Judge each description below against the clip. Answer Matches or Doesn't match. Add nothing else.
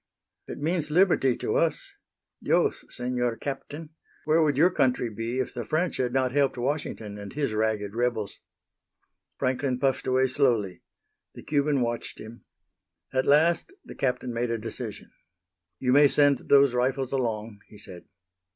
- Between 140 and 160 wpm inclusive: Matches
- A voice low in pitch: Matches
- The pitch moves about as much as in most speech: Matches